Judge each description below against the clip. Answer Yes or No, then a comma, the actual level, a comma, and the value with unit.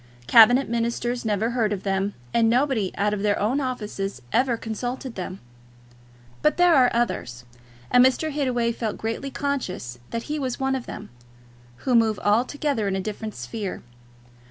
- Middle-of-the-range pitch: No, high, 230 Hz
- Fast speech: No, average, 160 wpm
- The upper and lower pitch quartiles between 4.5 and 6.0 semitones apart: No, average, 3.8 semitones